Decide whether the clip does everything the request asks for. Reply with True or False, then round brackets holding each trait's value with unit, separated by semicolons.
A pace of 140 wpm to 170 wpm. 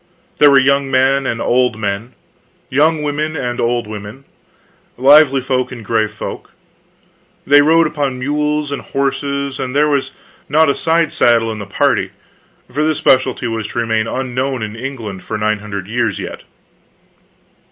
True (160 wpm)